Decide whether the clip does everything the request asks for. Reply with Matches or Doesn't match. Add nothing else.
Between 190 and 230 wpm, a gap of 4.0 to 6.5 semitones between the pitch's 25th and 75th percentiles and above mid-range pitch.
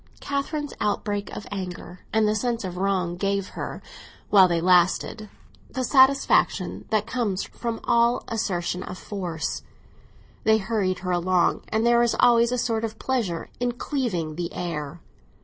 Doesn't match